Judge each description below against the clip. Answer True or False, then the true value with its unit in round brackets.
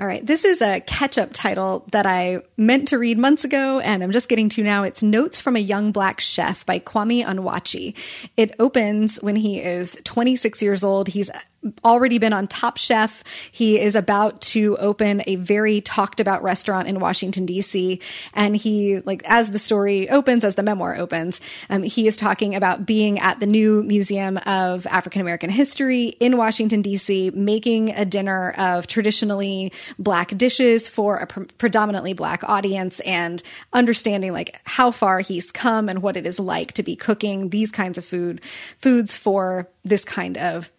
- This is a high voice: True (205 Hz)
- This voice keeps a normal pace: True (180 wpm)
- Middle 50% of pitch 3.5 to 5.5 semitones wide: False (2.7 semitones)